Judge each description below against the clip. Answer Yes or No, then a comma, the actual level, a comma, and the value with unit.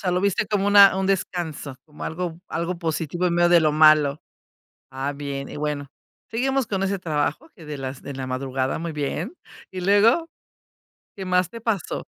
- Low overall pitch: No, medium, 170 Hz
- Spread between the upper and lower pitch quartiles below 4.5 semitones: No, average, 4.9 semitones